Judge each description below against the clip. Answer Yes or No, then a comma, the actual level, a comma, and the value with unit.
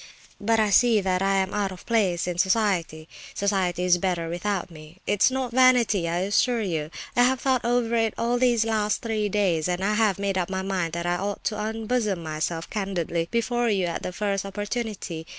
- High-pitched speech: Yes, high, 200 Hz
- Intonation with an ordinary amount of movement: Yes, average, 4.0 semitones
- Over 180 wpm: Yes, average, 200 wpm